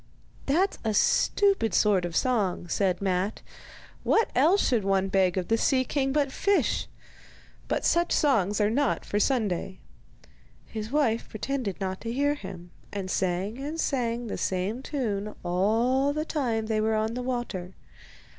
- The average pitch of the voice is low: No, high, 225 Hz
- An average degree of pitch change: No, wide, 5.7 semitones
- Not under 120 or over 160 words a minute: Yes, average, 155 wpm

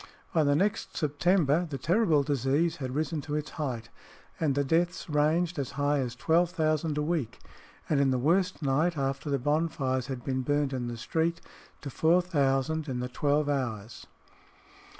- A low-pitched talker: No, medium, 145 Hz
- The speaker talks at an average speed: Yes, average, 170 wpm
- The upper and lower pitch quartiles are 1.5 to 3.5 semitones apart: Yes, average, 3.2 semitones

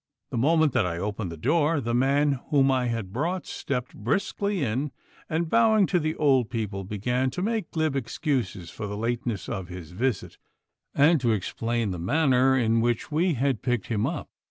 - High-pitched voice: No, low, 125 Hz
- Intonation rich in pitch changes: Yes, wide, 5.7 semitones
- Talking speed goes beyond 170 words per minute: Yes, average, 185 wpm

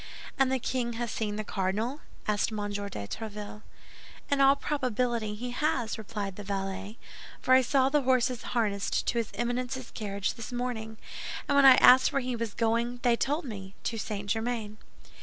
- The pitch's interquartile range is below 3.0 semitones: No, average, 3.3 semitones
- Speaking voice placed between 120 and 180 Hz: No, high, 230 Hz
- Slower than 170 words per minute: No, average, 175 wpm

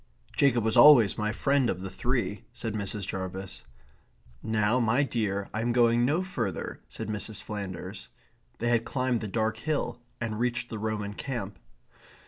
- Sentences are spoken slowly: No, average, 160 wpm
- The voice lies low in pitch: Yes, low, 110 Hz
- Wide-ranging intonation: No, average, 2.9 semitones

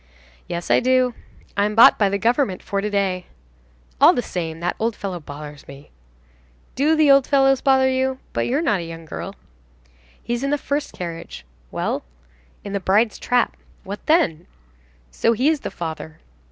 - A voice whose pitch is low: No, high, 210 Hz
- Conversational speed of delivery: Yes, average, 175 wpm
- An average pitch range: No, wide, 7.1 semitones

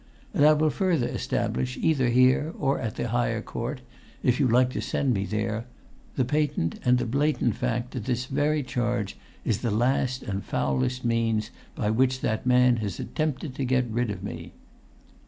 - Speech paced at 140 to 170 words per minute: No, average, 185 wpm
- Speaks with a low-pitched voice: Yes, low, 125 Hz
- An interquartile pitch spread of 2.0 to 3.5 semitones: Yes, average, 2.7 semitones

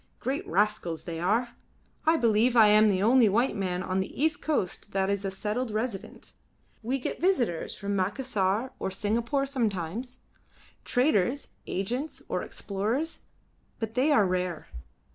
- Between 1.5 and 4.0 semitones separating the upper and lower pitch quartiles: No, average, 4.8 semitones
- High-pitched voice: Yes, high, 215 Hz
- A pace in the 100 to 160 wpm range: Yes, average, 145 wpm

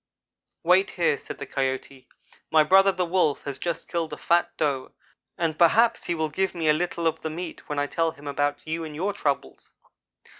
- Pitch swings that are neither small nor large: Yes, average, 3.1 semitones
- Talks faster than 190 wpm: Yes, average, 200 wpm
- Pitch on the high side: No, medium, 160 Hz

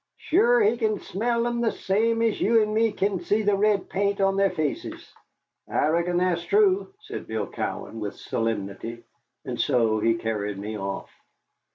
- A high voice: Yes, high, 195 Hz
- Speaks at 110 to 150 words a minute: No, average, 175 wpm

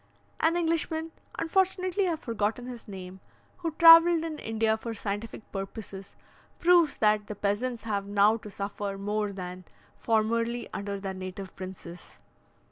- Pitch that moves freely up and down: Yes, wide, 8.0 semitones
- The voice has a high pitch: Yes, high, 220 Hz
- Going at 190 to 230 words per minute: No, average, 140 wpm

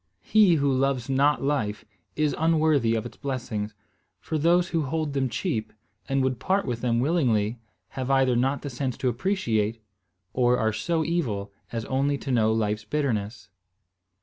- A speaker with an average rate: Yes, average, 165 wpm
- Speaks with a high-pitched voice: No, low, 130 Hz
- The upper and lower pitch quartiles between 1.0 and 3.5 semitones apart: No, average, 4.7 semitones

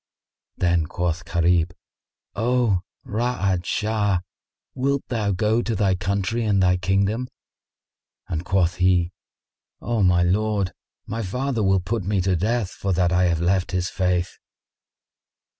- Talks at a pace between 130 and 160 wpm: Yes, slow, 135 wpm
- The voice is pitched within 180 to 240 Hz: No, very low, 95 Hz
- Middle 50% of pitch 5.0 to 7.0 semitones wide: No, average, 3.4 semitones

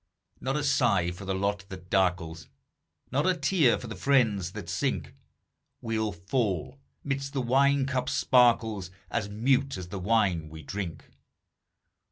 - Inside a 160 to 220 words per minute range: No, average, 150 wpm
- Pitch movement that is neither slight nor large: No, wide, 6.3 semitones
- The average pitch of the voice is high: No, low, 110 Hz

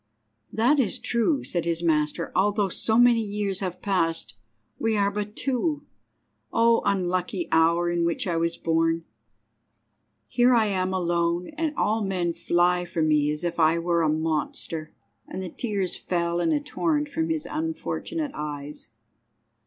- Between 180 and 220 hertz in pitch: Yes, medium, 185 Hz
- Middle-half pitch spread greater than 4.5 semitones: Yes, average, 5.2 semitones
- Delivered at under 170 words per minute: Yes, average, 155 wpm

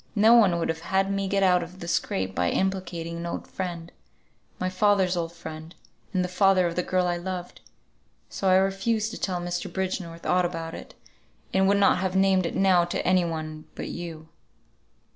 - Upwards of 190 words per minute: Yes, average, 200 wpm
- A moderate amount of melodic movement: No, narrow, 2.1 semitones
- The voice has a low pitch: No, medium, 180 Hz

